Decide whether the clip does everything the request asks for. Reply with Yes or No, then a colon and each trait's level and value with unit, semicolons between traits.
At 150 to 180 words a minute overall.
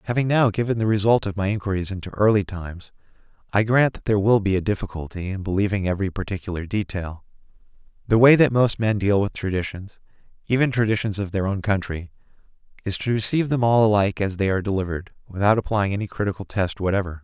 No: average, 190 wpm